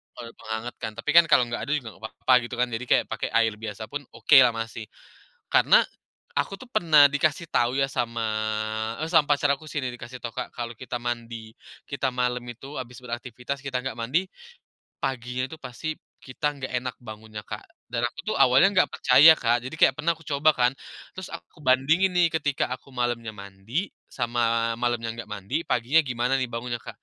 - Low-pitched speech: Yes, low, 125 Hz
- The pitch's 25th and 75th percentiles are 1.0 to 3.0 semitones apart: No, average, 3.6 semitones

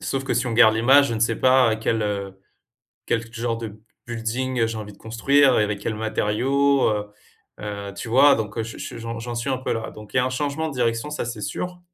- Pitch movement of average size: Yes, average, 3.0 semitones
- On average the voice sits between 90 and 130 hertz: Yes, low, 115 Hz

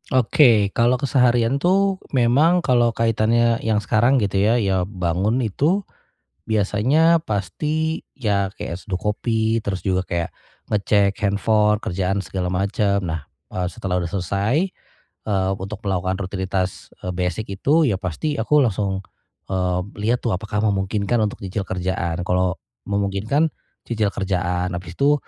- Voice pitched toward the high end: No, low, 100 Hz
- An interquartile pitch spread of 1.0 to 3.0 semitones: No, average, 4.1 semitones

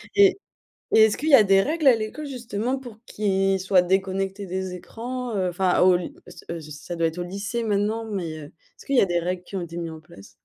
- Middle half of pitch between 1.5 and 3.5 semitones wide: No, average, 4.1 semitones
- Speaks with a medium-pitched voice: No, high, 195 Hz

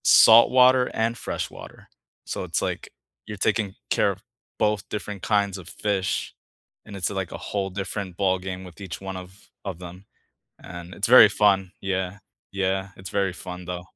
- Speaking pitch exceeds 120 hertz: No, very low, 95 Hz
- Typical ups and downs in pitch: No, narrow, 1.8 semitones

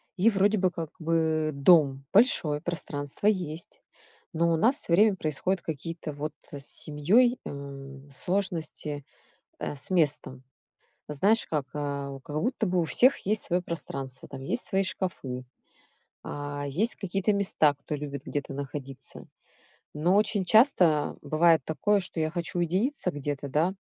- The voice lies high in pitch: No, medium, 160 Hz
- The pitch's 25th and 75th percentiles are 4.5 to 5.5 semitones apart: Yes, average, 4.8 semitones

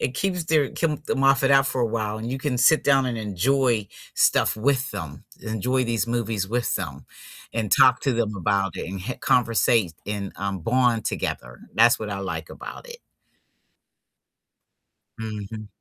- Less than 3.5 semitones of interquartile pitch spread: No, average, 4.2 semitones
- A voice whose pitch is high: No, low, 115 Hz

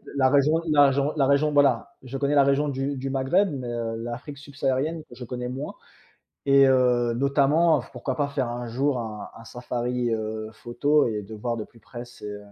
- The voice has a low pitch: Yes, low, 130 Hz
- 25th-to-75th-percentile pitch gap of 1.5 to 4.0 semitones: Yes, average, 3.0 semitones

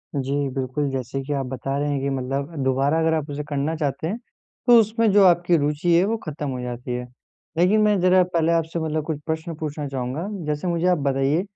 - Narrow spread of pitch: No, average, 3.8 semitones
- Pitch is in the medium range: Yes, medium, 150 Hz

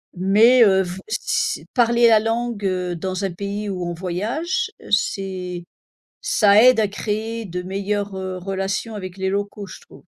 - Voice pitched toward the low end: No, high, 200 Hz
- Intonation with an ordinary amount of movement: Yes, average, 3.0 semitones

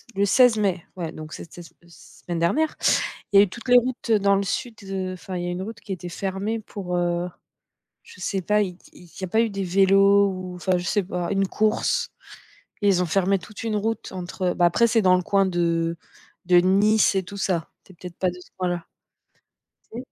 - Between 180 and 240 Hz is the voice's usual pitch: Yes, high, 190 Hz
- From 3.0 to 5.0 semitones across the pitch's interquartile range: No, narrow, 2.4 semitones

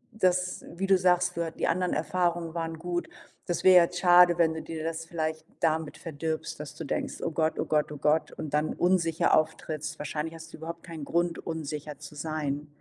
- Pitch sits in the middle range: Yes, medium, 165 Hz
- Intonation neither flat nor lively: No, narrow, 1.9 semitones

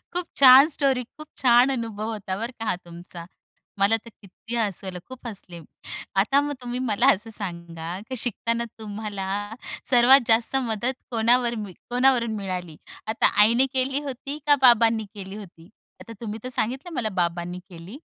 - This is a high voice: Yes, high, 225 Hz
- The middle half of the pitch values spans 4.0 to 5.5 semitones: Yes, average, 4.4 semitones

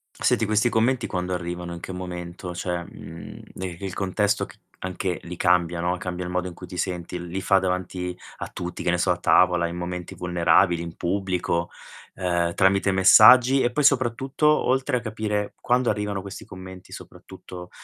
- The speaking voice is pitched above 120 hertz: No, very low, 90 Hz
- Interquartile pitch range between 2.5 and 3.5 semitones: Yes, average, 2.8 semitones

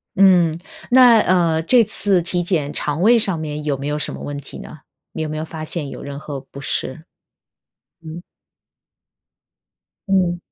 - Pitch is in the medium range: Yes, medium, 160 Hz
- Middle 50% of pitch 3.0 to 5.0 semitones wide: Yes, average, 3.8 semitones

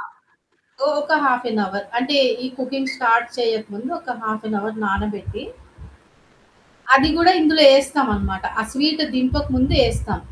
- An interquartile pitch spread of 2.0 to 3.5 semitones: No, average, 4.2 semitones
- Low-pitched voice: No, very high, 250 Hz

